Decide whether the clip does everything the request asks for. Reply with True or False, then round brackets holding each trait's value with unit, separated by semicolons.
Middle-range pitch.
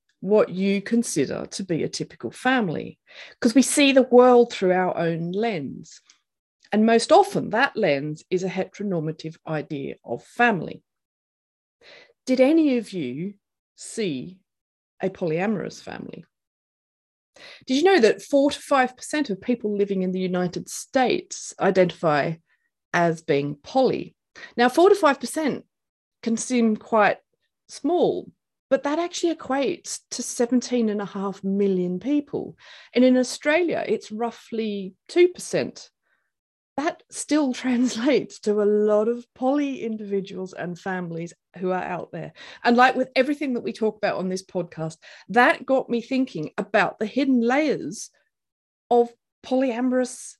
False (235 Hz)